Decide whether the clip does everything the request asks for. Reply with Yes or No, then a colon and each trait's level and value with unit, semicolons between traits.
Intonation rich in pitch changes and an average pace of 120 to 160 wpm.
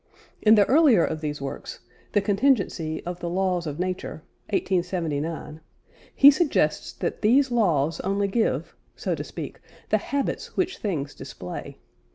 Yes: wide, 5.8 semitones; average, 145 wpm